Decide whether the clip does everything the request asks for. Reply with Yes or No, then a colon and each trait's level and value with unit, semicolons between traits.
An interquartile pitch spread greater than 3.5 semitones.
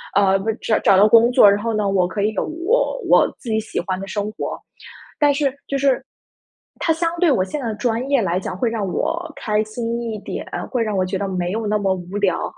Yes: average, 4.1 semitones